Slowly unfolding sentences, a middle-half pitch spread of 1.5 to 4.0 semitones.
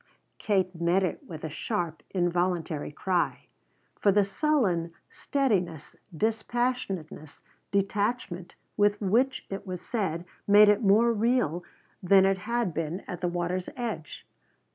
Yes: slow, 125 wpm; average, 3.7 semitones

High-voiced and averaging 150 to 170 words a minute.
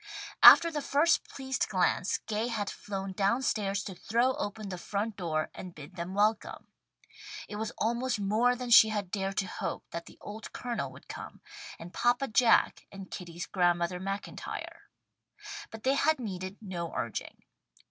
Yes: high, 205 Hz; average, 165 wpm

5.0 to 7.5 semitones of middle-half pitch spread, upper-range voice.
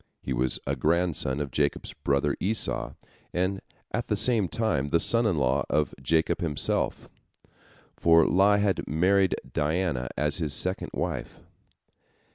No: average, 5.3 semitones; very low, 80 Hz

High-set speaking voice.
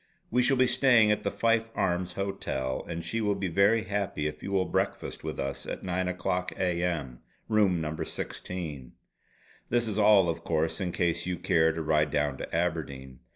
No: very low, 90 Hz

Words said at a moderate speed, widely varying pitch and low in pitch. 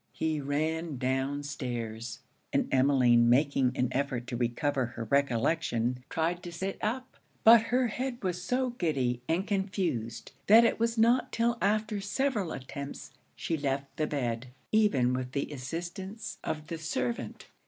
No: average, 150 wpm; wide, 7.8 semitones; medium, 150 Hz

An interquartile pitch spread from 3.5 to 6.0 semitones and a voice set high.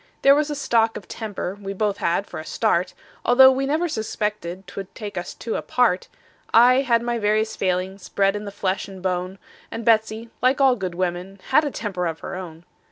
Yes: average, 4.1 semitones; high, 210 Hz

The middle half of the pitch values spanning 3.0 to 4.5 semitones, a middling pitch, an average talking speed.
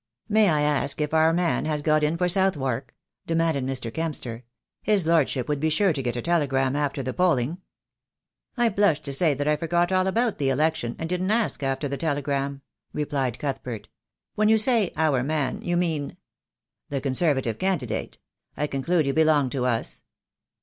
Yes: average, 4.1 semitones; medium, 150 Hz; average, 180 wpm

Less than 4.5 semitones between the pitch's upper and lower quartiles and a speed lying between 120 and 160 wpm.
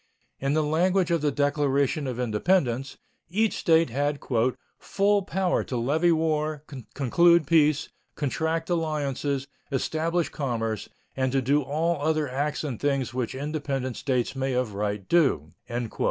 Yes: average, 3.6 semitones; average, 140 wpm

